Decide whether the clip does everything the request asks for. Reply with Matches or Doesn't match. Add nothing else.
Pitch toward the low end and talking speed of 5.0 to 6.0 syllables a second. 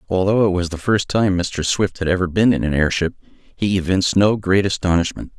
Matches